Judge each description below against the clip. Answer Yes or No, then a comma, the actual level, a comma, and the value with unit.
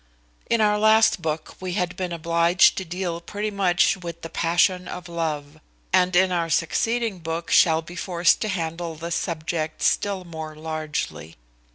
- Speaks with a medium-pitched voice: Yes, medium, 170 Hz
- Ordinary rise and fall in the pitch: No, narrow, 2.3 semitones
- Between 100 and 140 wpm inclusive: No, average, 165 wpm